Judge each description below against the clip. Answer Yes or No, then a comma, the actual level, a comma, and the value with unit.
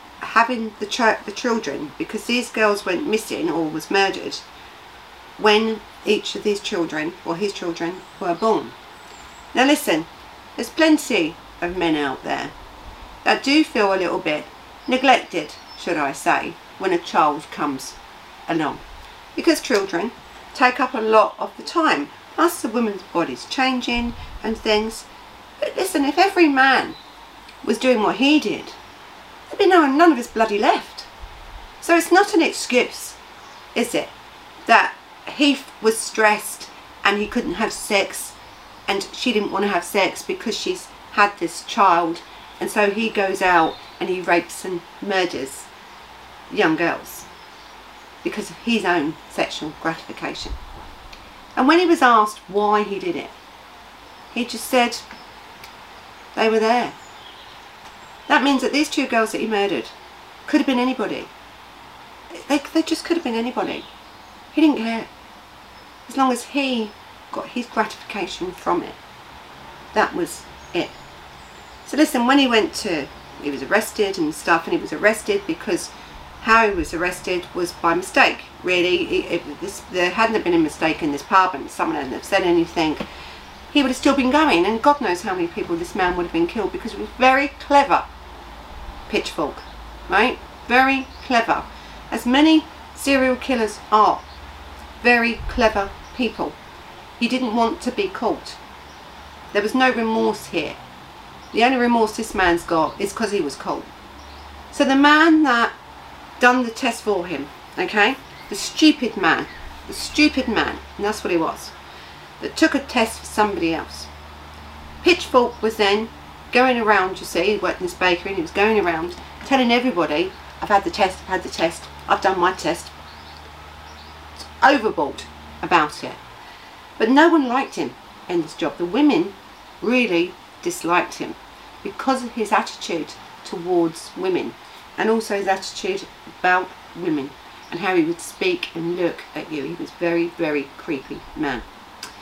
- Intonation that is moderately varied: No, wide, 6.7 semitones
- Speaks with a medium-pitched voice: No, high, 225 Hz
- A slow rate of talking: No, average, 160 wpm